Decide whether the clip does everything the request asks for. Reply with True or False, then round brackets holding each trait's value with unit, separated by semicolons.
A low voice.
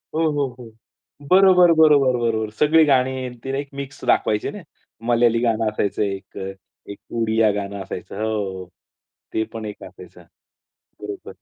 True (115 Hz)